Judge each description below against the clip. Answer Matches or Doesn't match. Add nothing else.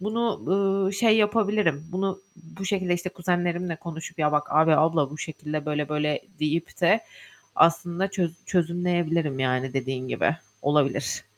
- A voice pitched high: Doesn't match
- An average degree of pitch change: Matches